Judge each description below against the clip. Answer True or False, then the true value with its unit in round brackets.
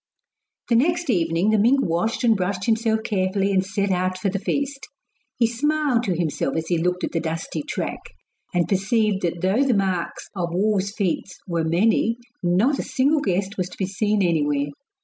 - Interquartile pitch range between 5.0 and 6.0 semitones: False (4.2 semitones)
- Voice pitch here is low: False (195 Hz)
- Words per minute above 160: True (190 wpm)